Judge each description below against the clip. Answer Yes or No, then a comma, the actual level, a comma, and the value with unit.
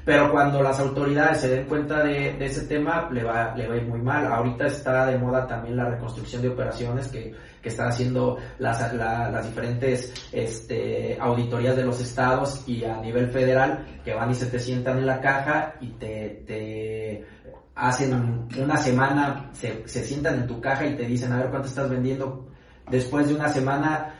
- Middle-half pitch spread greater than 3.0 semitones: No, narrow, 2.4 semitones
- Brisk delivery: Yes, fast, 195 wpm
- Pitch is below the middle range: Yes, low, 130 Hz